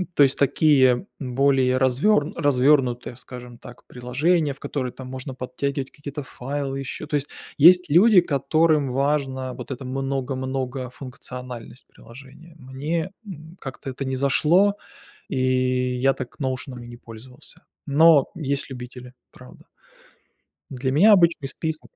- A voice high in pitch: No, low, 135 Hz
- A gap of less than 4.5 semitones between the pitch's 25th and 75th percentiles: Yes, average, 2.7 semitones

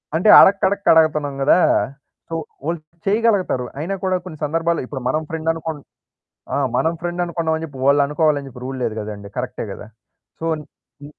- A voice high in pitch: No, medium, 160 Hz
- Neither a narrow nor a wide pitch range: Yes, average, 3.4 semitones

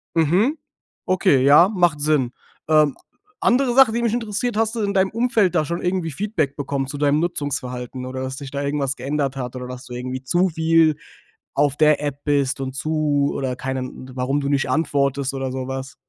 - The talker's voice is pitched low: No, medium, 145 Hz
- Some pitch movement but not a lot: Yes, average, 4.8 semitones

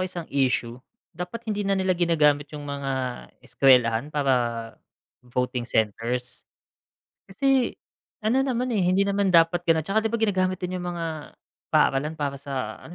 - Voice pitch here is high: No, medium, 165 Hz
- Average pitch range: No, wide, 6.1 semitones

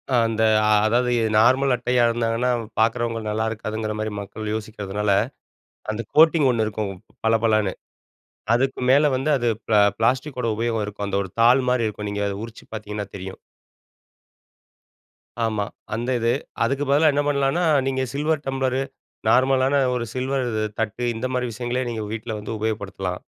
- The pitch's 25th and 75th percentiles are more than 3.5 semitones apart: No, average, 3.2 semitones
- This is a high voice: No, low, 115 Hz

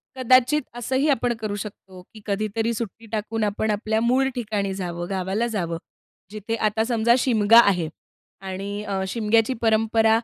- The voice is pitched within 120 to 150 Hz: No, high, 220 Hz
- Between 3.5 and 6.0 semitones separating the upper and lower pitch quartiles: No, narrow, 2.4 semitones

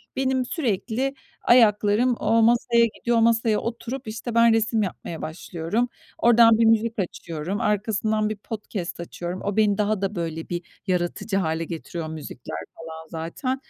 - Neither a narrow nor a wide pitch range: Yes, average, 5.0 semitones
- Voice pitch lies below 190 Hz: No, high, 215 Hz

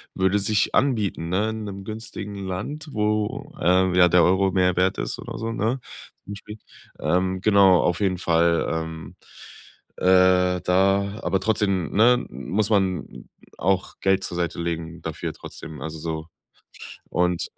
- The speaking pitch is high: No, very low, 95 Hz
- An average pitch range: Yes, average, 3.0 semitones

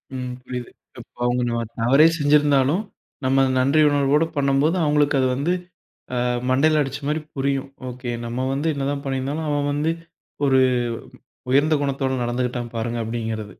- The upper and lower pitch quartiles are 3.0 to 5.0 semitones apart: No, narrow, 2.5 semitones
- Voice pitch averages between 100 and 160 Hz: Yes, low, 135 Hz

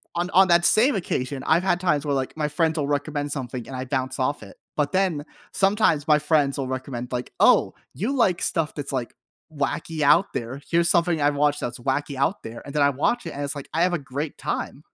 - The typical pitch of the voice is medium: Yes, medium, 145 Hz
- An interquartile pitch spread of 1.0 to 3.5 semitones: No, average, 3.9 semitones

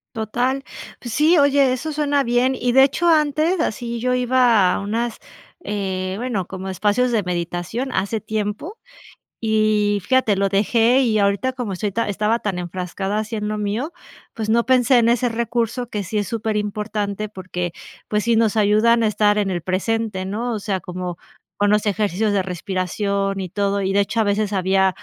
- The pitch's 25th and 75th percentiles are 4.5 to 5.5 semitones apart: No, average, 3.3 semitones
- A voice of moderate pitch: No, high, 215 Hz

